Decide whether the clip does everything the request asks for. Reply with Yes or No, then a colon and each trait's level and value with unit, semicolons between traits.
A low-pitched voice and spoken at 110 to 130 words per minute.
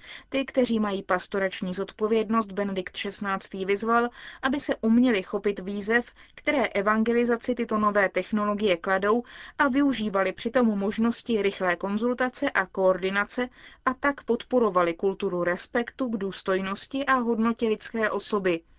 No: high, 215 Hz; average, 125 wpm